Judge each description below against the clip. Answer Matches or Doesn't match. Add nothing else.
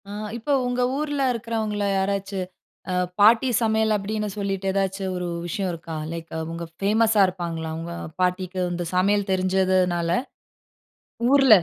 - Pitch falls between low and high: Doesn't match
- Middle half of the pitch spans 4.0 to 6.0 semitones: Doesn't match